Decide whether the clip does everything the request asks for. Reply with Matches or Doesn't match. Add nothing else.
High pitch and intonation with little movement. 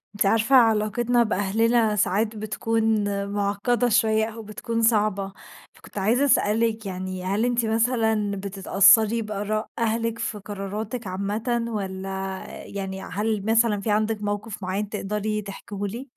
Matches